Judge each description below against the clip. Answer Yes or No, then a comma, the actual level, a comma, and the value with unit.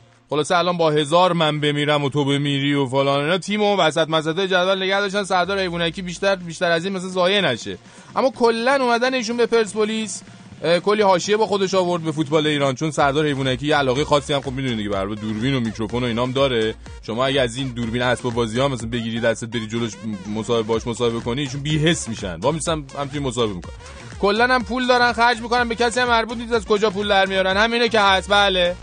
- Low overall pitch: No, medium, 160 Hz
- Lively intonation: Yes, wide, 8.0 semitones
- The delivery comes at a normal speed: No, fast, 220 wpm